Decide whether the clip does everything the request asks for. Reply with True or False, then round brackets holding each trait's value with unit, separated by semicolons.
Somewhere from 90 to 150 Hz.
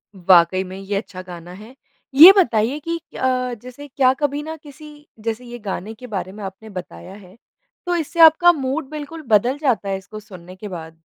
False (225 Hz)